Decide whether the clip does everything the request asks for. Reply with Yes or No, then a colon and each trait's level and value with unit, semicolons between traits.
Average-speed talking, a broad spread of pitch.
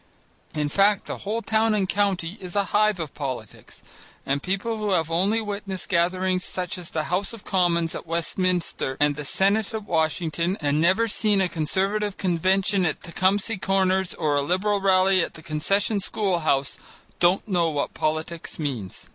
No: average, 170 wpm; average, 3.6 semitones